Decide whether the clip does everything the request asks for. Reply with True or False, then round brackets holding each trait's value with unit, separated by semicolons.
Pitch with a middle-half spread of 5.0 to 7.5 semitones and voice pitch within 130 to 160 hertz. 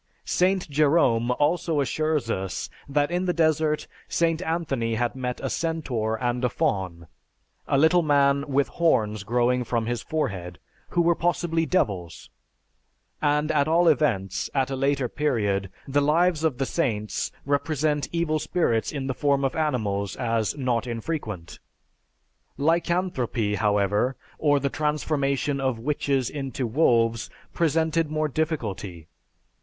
True (5.4 semitones; 140 Hz)